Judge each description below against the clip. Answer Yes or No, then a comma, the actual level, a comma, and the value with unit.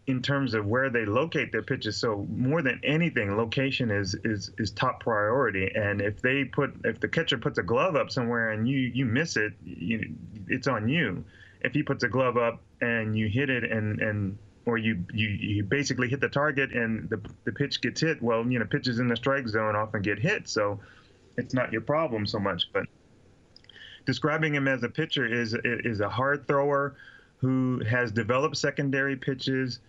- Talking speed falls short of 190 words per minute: No, average, 200 wpm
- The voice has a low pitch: Yes, low, 120 Hz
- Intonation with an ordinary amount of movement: Yes, average, 3.9 semitones